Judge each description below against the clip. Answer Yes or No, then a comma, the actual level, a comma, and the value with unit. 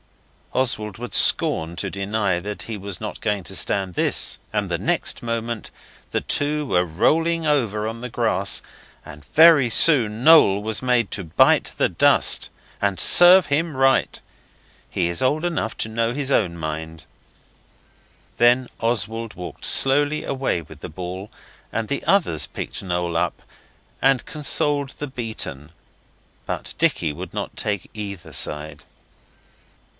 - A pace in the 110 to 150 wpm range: Yes, average, 145 wpm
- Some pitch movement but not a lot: No, wide, 6.6 semitones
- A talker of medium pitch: No, low, 110 Hz